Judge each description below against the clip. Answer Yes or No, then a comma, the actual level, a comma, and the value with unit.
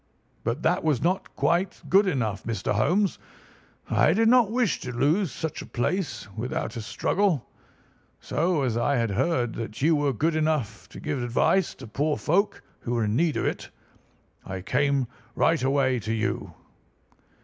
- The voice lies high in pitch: No, medium, 140 Hz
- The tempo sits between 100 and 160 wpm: No, average, 170 wpm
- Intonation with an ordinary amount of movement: No, wide, 6.5 semitones